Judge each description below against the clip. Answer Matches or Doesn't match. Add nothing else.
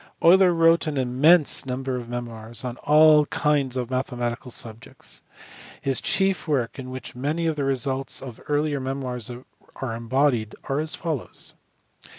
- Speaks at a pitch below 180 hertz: Matches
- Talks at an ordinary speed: Matches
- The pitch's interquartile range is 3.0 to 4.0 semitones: Matches